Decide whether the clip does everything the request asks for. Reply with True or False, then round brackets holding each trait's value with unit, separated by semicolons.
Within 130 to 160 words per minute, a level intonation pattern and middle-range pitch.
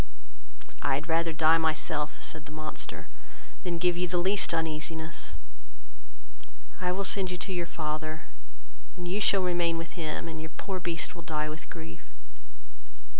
True (150 wpm; 2.2 semitones; 165 Hz)